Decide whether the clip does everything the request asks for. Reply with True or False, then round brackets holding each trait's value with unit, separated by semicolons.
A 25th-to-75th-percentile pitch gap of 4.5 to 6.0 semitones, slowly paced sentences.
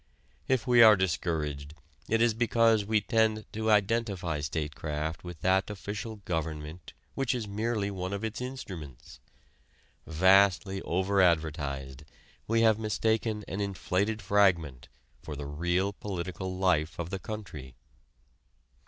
True (5.2 semitones; 125 wpm)